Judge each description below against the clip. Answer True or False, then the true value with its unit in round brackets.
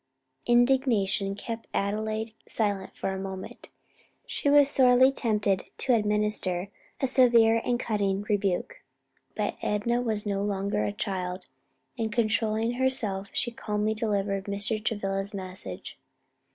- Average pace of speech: False (125 wpm)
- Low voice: False (210 Hz)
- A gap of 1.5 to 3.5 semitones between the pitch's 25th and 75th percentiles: True (3.0 semitones)